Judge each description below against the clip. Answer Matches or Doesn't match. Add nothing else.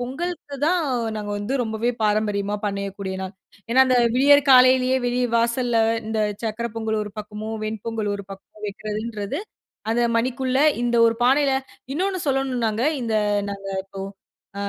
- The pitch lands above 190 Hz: Matches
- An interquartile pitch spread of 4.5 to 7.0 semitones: Doesn't match